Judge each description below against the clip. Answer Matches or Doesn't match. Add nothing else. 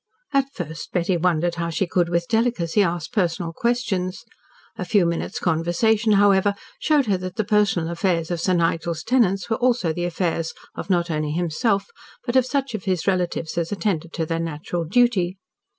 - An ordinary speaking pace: Matches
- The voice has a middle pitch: Matches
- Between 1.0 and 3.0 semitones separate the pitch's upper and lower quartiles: Doesn't match